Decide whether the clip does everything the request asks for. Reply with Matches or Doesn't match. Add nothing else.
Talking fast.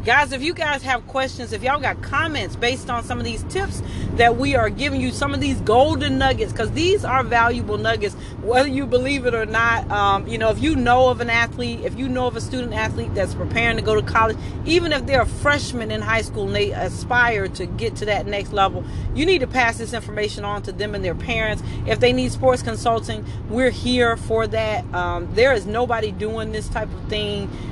Matches